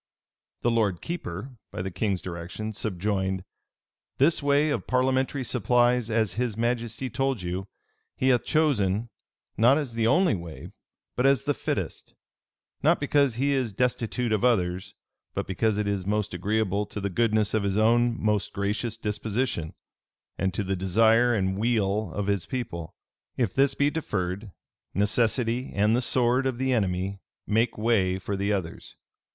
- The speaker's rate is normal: Yes, average, 160 wpm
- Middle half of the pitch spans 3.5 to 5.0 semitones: Yes, average, 4.1 semitones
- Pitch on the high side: No, low, 110 Hz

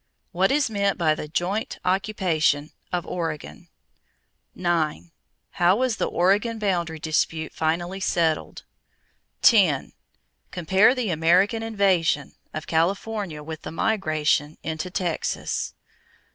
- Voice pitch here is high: No, medium, 175 Hz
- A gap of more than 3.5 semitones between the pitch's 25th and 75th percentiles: Yes, average, 4.0 semitones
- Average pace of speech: No, slow, 110 wpm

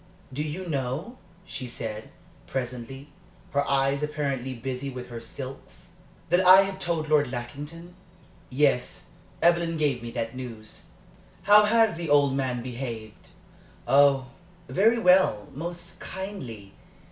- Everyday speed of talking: No, slow, 125 wpm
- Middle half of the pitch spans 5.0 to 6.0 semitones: Yes, wide, 5.4 semitones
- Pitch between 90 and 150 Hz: Yes, medium, 140 Hz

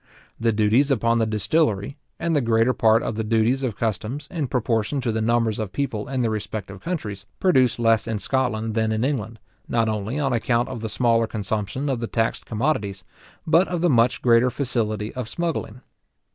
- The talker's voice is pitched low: Yes, low, 115 Hz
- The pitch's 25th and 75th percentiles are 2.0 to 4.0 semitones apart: Yes, average, 3.2 semitones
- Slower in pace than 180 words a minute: No, average, 190 wpm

